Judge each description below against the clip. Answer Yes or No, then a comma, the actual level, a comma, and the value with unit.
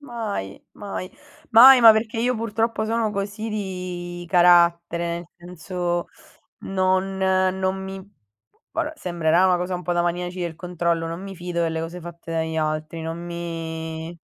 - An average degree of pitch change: No, narrow, 2.2 semitones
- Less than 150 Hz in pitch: No, medium, 180 Hz